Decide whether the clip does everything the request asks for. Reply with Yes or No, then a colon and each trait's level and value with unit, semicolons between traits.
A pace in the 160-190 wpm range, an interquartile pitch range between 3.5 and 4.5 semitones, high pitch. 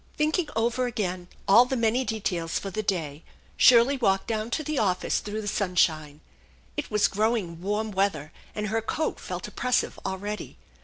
Yes: average, 165 wpm; average, 4.1 semitones; high, 210 Hz